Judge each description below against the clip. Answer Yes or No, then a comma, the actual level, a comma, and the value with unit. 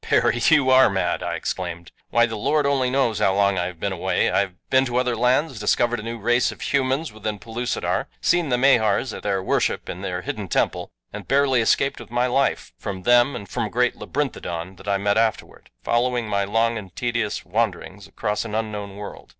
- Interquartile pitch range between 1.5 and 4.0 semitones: Yes, average, 3.7 semitones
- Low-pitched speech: Yes, low, 115 Hz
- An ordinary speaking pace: No, fast, 210 wpm